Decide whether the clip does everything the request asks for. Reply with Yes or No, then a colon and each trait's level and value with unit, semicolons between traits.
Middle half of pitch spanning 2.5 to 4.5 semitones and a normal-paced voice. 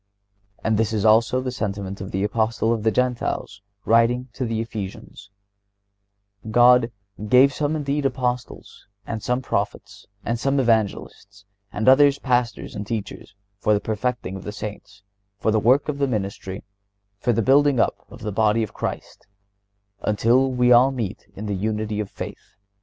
Yes: average, 3.3 semitones; average, 165 wpm